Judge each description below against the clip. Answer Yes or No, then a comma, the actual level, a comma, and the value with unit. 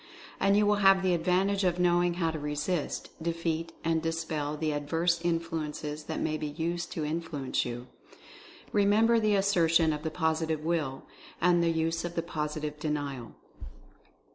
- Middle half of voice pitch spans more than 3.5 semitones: No, narrow, 2.5 semitones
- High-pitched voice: No, medium, 165 Hz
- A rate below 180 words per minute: Yes, average, 160 wpm